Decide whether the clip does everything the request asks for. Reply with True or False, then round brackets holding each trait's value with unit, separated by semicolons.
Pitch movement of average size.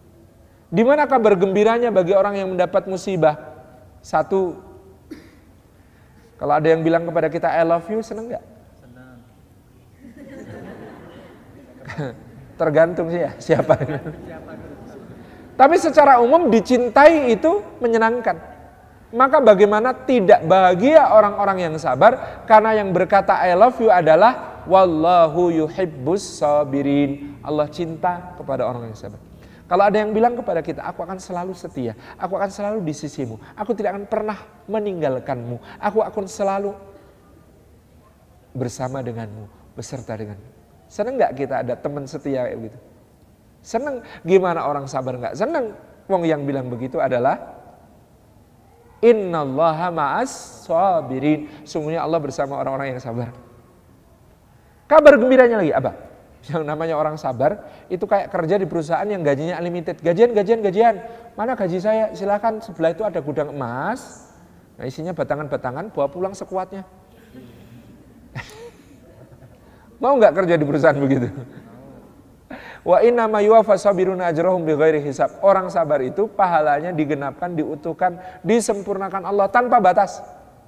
False (6.8 semitones)